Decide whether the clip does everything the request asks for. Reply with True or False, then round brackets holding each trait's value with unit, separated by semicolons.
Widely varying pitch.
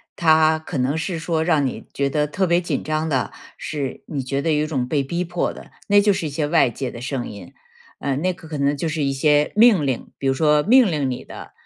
False (3.1 semitones)